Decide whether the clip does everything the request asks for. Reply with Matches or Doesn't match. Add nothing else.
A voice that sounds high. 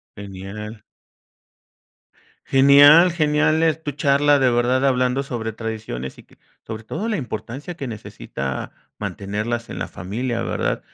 Doesn't match